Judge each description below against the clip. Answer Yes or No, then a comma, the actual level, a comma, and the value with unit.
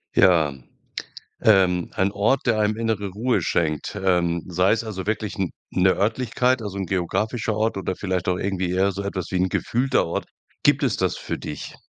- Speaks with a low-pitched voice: Yes, very low, 95 Hz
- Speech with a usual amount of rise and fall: Yes, average, 3.1 semitones